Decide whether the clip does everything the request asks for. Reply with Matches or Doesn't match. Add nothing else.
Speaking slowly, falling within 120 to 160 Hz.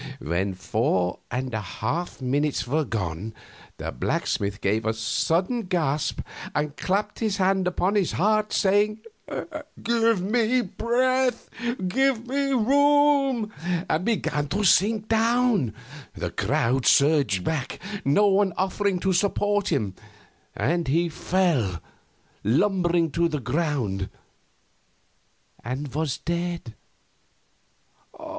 Doesn't match